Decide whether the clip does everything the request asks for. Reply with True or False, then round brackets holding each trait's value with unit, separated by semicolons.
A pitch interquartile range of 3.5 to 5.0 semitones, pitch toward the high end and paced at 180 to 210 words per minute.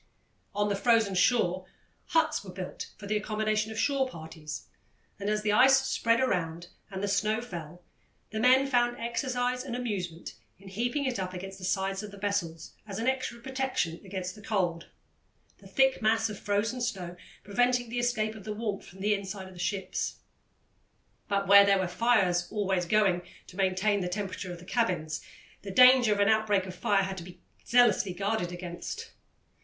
True (4.0 semitones; 205 Hz; 185 wpm)